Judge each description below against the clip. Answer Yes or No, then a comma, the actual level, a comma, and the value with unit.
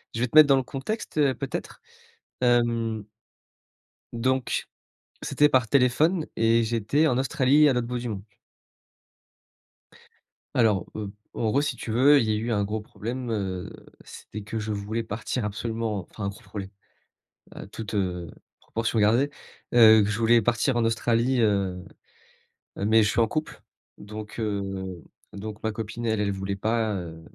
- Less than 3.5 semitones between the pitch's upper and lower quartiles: Yes, average, 2.8 semitones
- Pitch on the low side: Yes, low, 110 Hz